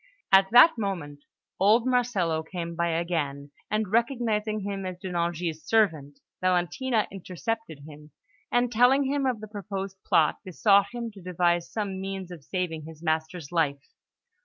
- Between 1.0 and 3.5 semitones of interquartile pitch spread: No, average, 4.5 semitones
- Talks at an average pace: Yes, average, 150 wpm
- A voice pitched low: No, high, 190 Hz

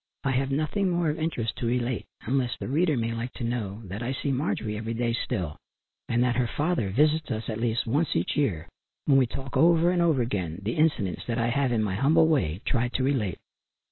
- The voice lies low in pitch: Yes, low, 125 Hz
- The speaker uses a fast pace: Yes, fast, 225 wpm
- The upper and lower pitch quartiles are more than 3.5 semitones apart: Yes, average, 4.6 semitones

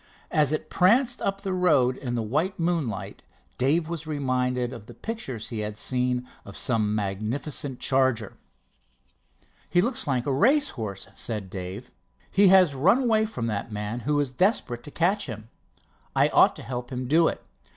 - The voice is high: No, low, 130 Hz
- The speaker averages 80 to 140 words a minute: No, average, 170 wpm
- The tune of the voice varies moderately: No, wide, 7.3 semitones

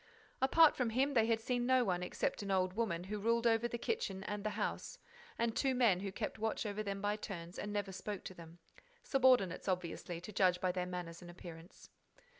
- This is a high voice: Yes, high, 205 Hz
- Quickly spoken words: Yes, fast, 215 wpm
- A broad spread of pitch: No, average, 4.3 semitones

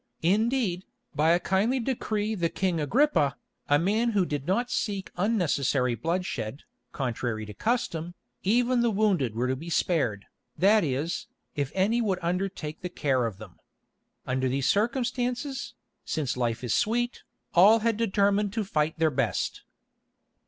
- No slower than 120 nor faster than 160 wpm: Yes, average, 145 wpm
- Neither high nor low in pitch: Yes, medium, 180 Hz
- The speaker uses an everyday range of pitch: No, wide, 7.7 semitones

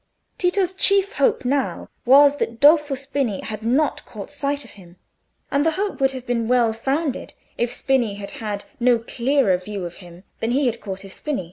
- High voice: Yes, very high, 250 Hz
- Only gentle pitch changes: No, average, 4.7 semitones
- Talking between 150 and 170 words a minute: No, average, 195 wpm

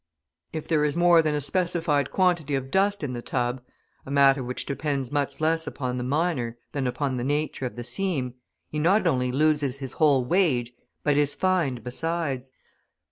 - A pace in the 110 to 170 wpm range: No, average, 185 wpm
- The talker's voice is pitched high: No, medium, 145 Hz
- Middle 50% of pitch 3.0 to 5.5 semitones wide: Yes, average, 4.1 semitones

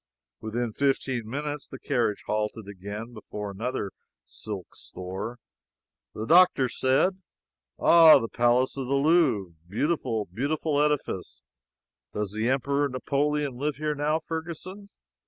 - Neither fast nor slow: No, slow, 125 wpm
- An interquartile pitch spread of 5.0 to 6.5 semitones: Yes, wide, 5.4 semitones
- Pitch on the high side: No, low, 130 Hz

